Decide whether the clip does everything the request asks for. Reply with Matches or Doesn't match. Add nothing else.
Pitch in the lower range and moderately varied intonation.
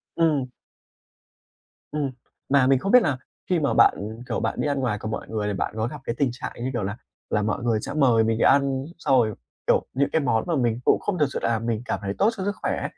Matches